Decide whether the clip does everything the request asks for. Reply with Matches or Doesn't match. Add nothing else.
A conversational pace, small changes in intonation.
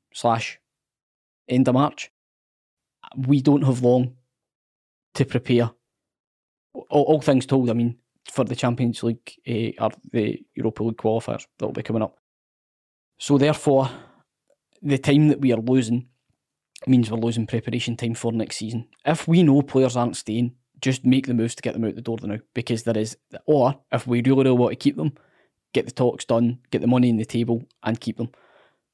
Matches